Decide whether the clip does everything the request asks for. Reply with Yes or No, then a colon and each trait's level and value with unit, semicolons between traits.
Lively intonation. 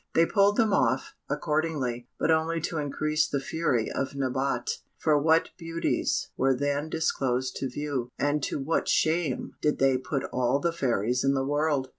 No: average, 3.4 semitones